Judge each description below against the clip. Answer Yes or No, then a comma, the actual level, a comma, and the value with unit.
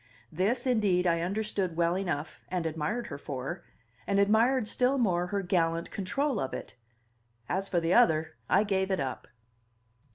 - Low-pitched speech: No, medium, 185 Hz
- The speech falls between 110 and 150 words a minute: No, average, 160 wpm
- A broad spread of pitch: No, average, 4.2 semitones